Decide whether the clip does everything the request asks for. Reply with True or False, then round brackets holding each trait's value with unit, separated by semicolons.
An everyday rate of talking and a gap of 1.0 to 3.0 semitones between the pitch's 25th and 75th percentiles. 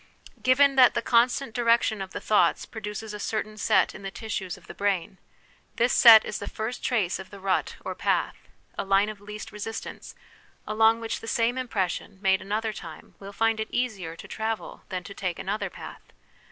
True (195 wpm; 2.6 semitones)